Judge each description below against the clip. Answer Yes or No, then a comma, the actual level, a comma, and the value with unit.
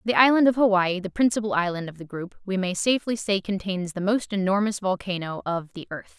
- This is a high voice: Yes, high, 195 Hz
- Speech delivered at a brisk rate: Yes, fast, 215 wpm